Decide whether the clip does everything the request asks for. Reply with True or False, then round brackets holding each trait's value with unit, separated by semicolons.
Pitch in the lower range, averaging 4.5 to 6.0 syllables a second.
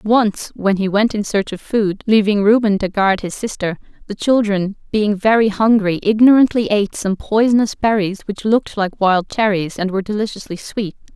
False (205 Hz; 5.0 syllables/s)